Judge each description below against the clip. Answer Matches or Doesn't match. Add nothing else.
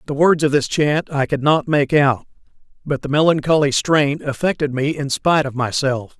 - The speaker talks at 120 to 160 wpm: Doesn't match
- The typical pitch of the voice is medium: Matches